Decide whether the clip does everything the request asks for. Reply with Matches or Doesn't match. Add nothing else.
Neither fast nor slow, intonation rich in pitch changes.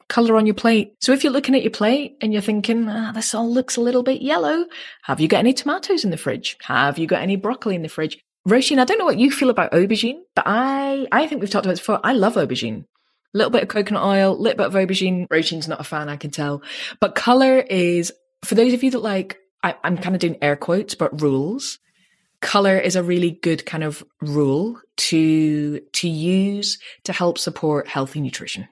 Doesn't match